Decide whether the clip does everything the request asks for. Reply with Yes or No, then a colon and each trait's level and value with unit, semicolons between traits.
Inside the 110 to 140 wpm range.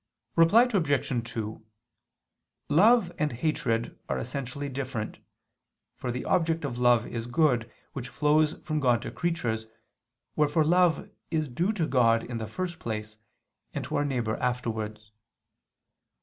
Yes: slow, 135 wpm